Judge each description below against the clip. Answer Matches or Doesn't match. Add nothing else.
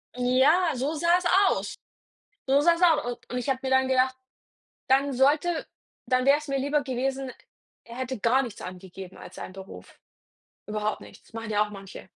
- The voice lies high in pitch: Matches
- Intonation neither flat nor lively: Matches